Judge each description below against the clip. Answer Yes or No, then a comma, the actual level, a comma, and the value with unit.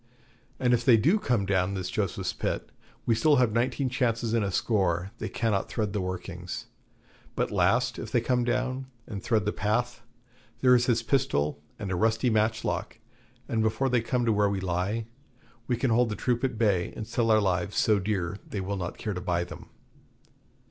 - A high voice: No, low, 110 Hz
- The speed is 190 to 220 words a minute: Yes, average, 195 wpm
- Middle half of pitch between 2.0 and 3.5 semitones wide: No, average, 3.9 semitones